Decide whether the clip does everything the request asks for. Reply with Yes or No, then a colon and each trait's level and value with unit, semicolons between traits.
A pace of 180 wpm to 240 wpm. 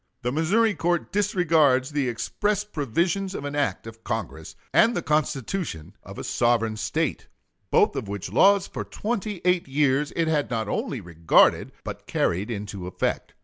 No: average, 160 wpm